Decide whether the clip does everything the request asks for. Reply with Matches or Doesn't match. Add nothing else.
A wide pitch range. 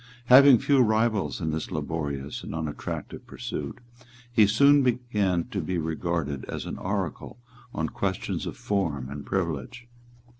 Matches